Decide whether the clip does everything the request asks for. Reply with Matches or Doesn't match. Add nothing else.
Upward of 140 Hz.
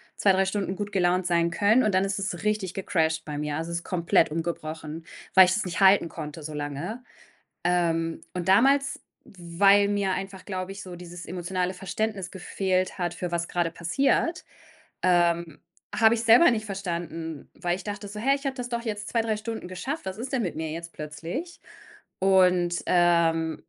Matches